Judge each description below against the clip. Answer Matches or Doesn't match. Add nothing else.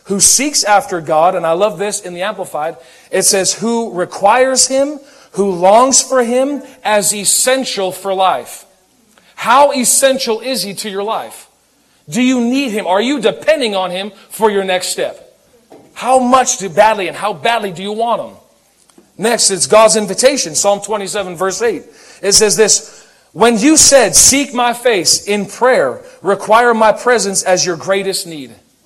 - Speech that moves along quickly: Doesn't match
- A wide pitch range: Doesn't match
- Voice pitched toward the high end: Matches